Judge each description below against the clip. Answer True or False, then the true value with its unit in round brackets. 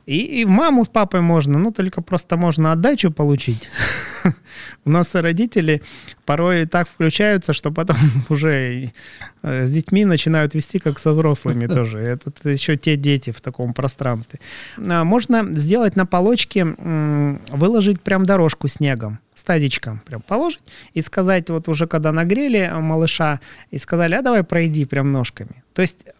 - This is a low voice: False (160 Hz)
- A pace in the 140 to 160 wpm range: True (145 wpm)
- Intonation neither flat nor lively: True (4.7 semitones)